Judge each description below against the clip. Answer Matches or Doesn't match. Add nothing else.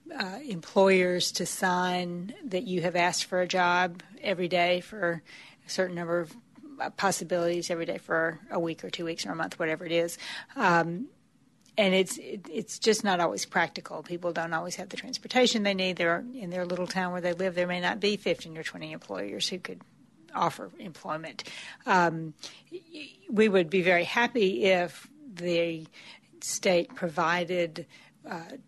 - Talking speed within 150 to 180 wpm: Matches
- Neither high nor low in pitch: Matches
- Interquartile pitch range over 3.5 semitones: Doesn't match